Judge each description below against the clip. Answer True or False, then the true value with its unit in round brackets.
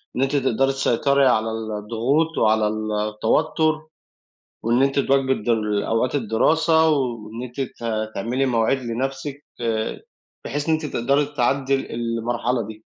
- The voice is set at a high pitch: False (125 Hz)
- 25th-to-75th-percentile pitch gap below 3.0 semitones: False (3.5 semitones)